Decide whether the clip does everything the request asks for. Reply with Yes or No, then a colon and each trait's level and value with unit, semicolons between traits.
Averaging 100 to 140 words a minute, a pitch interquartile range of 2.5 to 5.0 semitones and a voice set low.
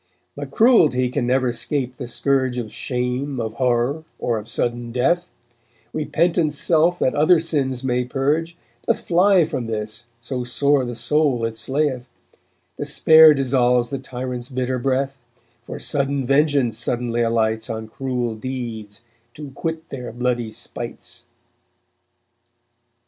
Yes: slow, 135 wpm; average, 3.2 semitones; low, 130 Hz